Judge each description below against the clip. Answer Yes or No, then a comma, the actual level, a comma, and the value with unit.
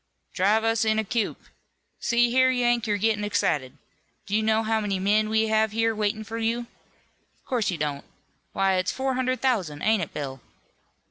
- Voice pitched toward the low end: No, high, 220 Hz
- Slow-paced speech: No, average, 190 wpm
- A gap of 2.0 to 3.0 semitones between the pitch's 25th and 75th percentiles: Yes, narrow, 2.6 semitones